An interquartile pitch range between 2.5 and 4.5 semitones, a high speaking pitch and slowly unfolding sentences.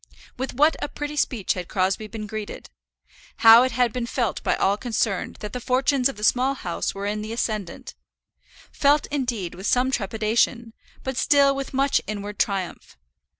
No: average, 4.1 semitones; high, 230 Hz; average, 175 wpm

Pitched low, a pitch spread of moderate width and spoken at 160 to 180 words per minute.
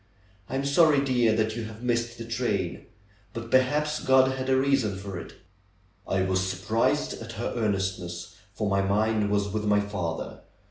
Yes: low, 110 Hz; average, 4.5 semitones; average, 175 wpm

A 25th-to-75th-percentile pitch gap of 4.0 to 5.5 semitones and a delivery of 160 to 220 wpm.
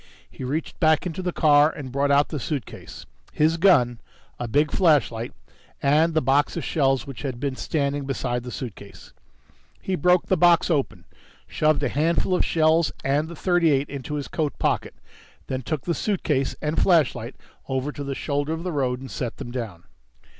No: average, 3.3 semitones; average, 180 wpm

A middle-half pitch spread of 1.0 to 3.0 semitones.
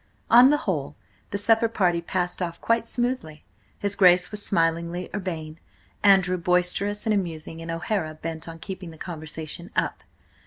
No: average, 3.6 semitones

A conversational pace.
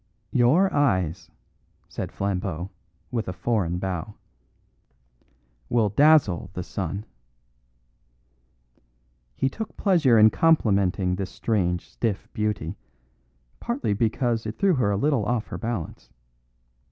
No: slow, 110 wpm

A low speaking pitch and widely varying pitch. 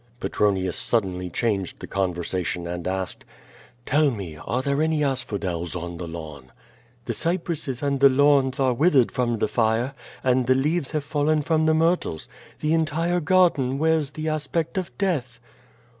Yes: low, 130 Hz; wide, 8.0 semitones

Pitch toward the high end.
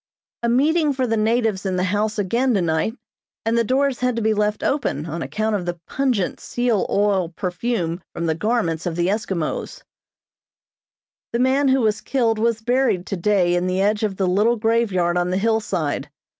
Yes: high, 215 Hz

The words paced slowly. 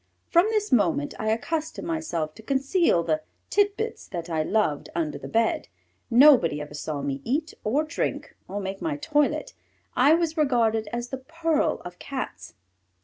No: average, 160 wpm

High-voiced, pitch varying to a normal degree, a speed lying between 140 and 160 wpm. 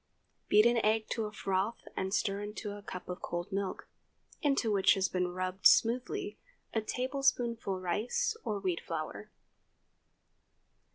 Yes: high, 205 Hz; average, 3.8 semitones; average, 145 wpm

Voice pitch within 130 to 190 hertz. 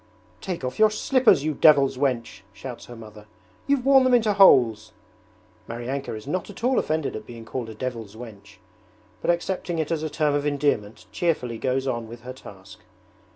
Yes: low, 135 Hz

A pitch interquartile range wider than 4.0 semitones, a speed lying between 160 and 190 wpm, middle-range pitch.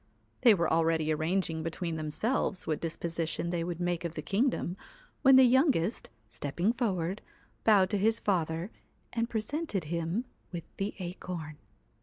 No: average, 4.7 semitones; average, 145 wpm; medium, 175 Hz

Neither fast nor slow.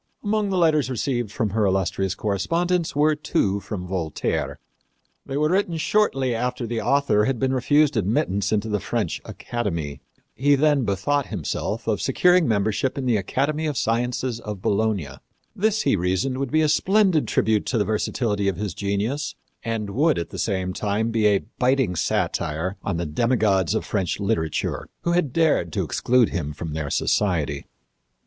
Yes: average, 170 wpm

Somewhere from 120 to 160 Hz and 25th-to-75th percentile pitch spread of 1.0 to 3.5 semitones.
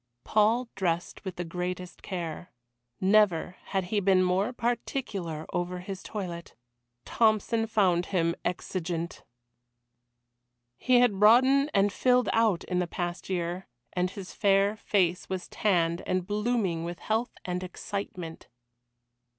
No: medium, 185 Hz; average, 3.2 semitones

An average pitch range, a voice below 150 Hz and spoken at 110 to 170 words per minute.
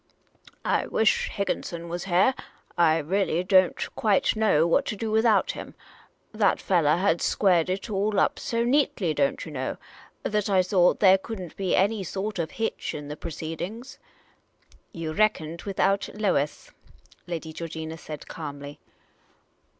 No: average, 4.2 semitones; medium, 185 Hz; average, 150 wpm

